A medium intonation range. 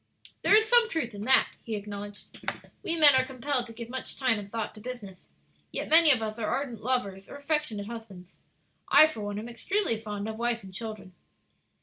Yes: average, 4.4 semitones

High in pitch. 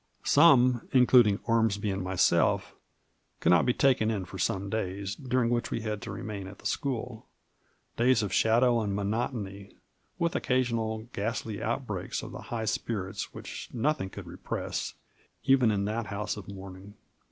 No: low, 110 Hz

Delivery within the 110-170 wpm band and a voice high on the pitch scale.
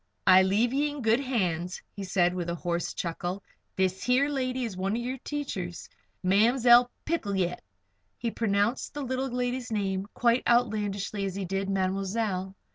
Yes: average, 165 wpm; high, 205 Hz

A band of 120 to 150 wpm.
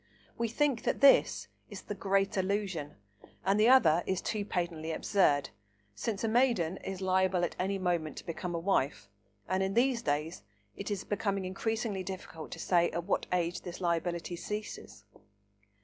No: average, 165 wpm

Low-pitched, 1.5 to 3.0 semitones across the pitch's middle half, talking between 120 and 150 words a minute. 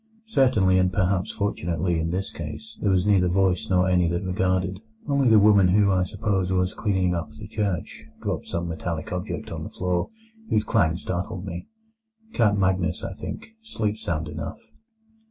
No: very low, 95 Hz; narrow, 2.6 semitones; average, 170 wpm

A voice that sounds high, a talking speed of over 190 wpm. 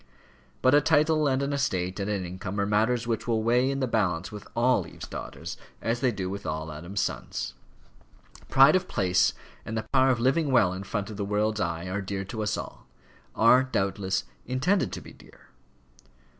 No: low, 110 Hz; average, 200 wpm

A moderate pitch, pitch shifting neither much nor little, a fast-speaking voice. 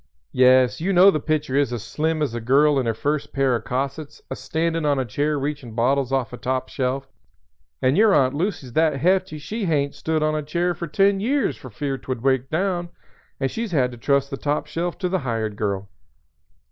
Yes: medium, 145 Hz; average, 4.0 semitones; fast, 220 wpm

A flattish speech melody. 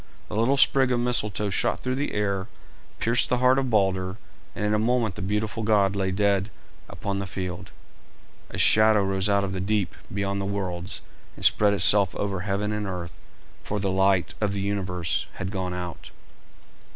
Yes: narrow, 1.9 semitones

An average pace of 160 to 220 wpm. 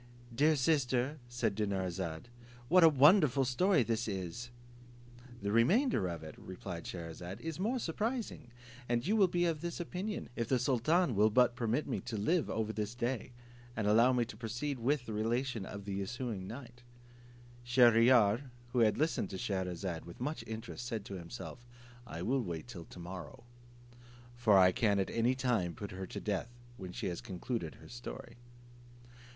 Yes: average, 170 wpm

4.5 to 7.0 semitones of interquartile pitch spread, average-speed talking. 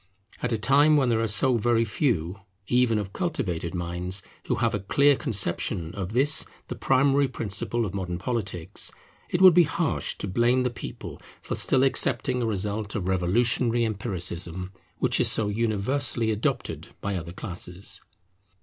Yes: average, 4.9 semitones; average, 160 wpm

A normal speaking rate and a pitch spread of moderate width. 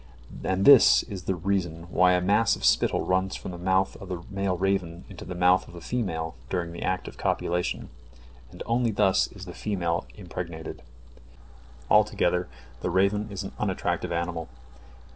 No: average, 170 wpm; narrow, 2.0 semitones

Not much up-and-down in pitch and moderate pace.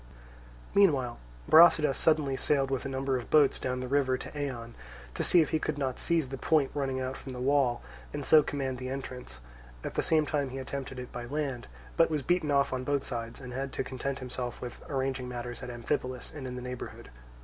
No: narrow, 2.2 semitones; fast, 215 wpm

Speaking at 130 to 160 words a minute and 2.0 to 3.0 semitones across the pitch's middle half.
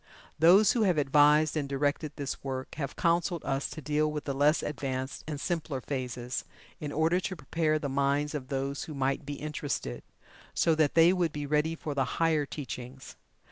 No: average, 185 wpm; narrow, 2.5 semitones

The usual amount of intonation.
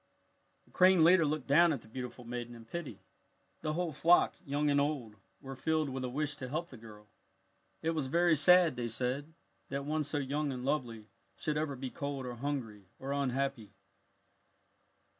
Yes: average, 3.7 semitones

